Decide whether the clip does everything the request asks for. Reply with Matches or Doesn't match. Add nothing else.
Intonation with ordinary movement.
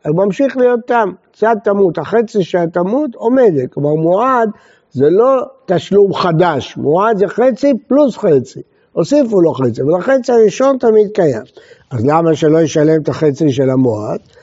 Doesn't match